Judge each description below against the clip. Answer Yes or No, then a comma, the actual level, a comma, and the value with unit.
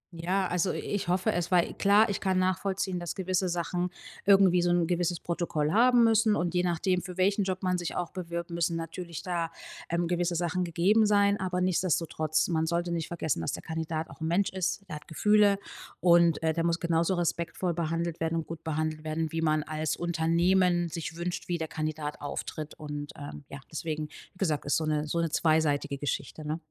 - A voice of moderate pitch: Yes, medium, 170 Hz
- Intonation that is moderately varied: No, narrow, 2.3 semitones